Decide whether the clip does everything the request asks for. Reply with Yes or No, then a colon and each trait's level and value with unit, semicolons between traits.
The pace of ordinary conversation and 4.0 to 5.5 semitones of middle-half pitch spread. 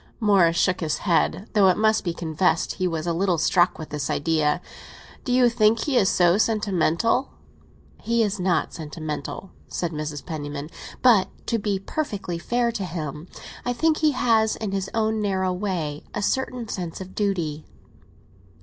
Yes: average, 170 wpm; average, 4.9 semitones